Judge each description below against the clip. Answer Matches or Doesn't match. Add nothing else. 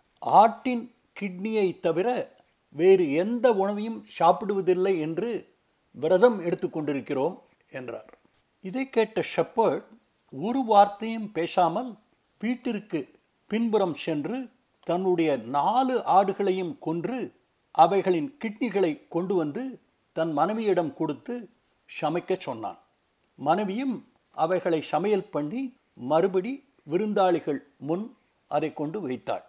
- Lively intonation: Matches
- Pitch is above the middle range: Matches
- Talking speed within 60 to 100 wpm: Matches